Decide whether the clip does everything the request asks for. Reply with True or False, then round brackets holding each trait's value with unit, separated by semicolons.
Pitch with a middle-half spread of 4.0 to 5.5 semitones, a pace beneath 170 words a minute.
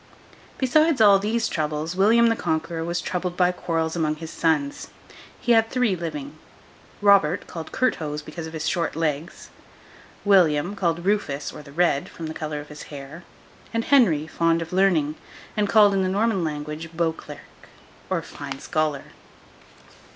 True (4.5 semitones; 160 wpm)